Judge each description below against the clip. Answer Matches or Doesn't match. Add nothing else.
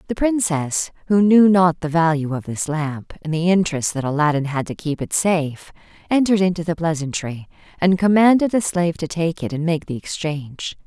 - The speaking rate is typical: Matches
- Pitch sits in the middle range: Matches